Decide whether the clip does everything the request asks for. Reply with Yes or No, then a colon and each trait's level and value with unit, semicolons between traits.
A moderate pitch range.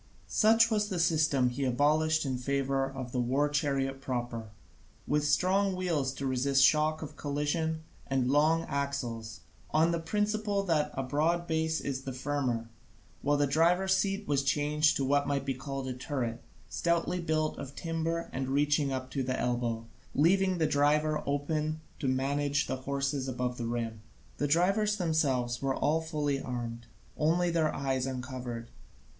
Yes: average, 3.5 semitones